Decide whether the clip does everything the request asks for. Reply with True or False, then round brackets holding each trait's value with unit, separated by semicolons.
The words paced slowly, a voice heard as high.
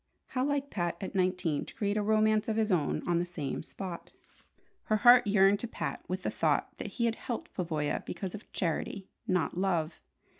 False (195 wpm; 195 Hz)